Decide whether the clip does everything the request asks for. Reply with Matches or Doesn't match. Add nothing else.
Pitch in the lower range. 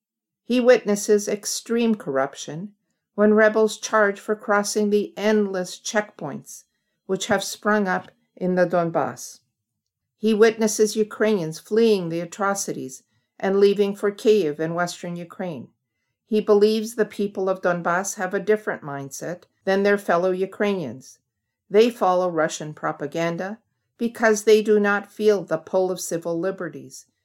Doesn't match